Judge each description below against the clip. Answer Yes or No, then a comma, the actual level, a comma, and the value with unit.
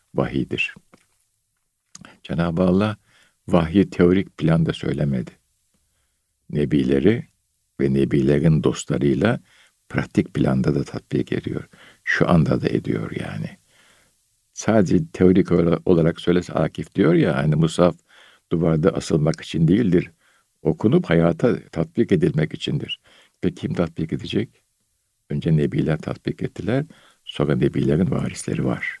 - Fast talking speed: No, average, 105 wpm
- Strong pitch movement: No, average, 3.5 semitones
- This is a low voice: Yes, very low, 85 Hz